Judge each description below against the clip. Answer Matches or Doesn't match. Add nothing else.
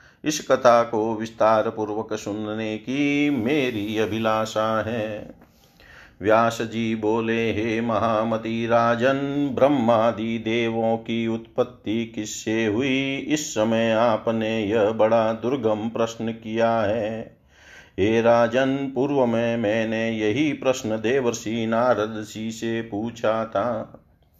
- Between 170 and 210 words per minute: Doesn't match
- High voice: Doesn't match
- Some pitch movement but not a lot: Doesn't match